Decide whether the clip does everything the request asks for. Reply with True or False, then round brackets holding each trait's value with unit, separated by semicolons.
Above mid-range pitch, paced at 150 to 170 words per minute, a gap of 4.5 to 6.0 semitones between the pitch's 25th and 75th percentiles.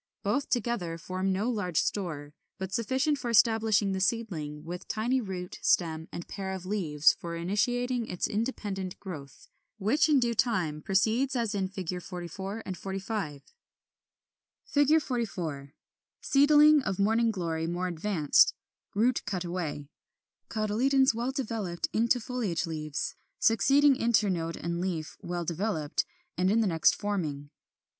False (195 Hz; 135 wpm; 5.2 semitones)